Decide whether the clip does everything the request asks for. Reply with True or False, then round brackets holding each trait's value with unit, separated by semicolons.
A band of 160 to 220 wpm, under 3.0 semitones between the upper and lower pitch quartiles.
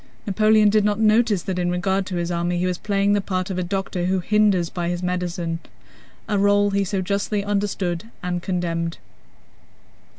True (175 wpm; 2.5 semitones)